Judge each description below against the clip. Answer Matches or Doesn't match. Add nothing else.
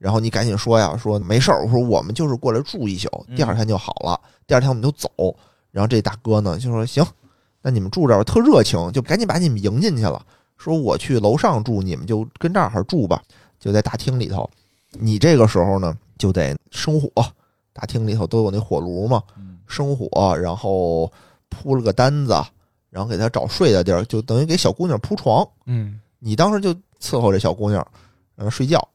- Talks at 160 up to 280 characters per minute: Doesn't match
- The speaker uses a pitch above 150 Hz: Doesn't match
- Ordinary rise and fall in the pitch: Matches